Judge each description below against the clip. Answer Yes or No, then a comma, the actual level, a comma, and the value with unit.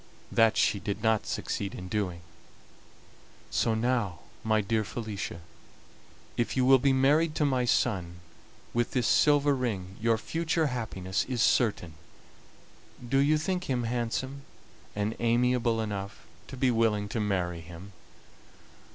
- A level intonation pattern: No, average, 4.2 semitones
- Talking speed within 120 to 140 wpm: Yes, slow, 135 wpm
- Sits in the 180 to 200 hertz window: No, low, 115 Hz